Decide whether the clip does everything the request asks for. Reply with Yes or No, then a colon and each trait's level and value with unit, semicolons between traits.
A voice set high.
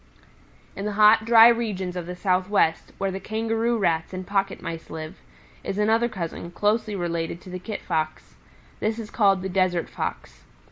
Yes: high, 195 Hz